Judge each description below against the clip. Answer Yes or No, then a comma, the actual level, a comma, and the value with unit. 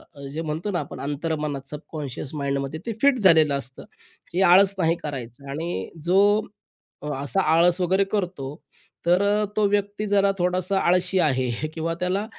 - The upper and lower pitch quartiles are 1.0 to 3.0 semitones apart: No, average, 5.0 semitones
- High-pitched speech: No, medium, 170 Hz